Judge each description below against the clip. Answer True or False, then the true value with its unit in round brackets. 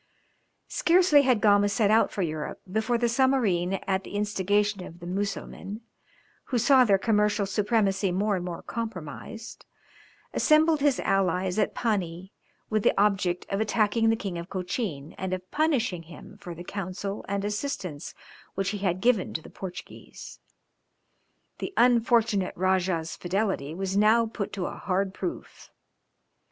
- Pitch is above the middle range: True (200 Hz)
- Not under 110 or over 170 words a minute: True (150 wpm)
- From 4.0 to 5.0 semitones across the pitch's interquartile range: False (3.4 semitones)